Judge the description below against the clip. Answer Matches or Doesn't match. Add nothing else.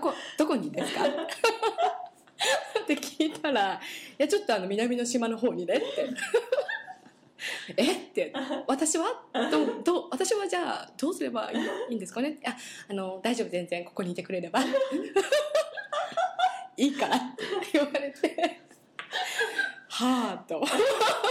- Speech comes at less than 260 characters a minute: Matches